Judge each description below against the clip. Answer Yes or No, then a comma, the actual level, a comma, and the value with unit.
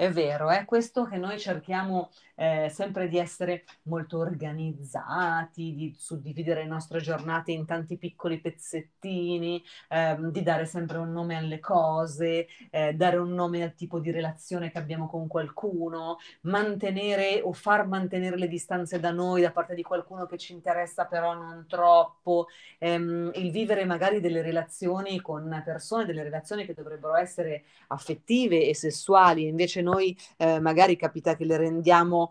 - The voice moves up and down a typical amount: No, narrow, 1.8 semitones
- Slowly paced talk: No, average, 155 wpm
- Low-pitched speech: No, medium, 170 Hz